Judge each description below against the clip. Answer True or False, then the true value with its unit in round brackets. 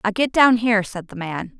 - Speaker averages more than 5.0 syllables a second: True (5.4 syllables/s)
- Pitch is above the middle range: True (210 Hz)